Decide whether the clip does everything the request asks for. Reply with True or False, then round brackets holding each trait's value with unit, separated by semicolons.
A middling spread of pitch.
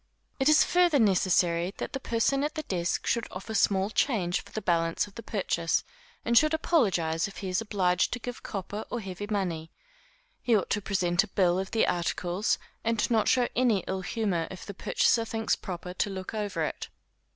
True (4.2 semitones)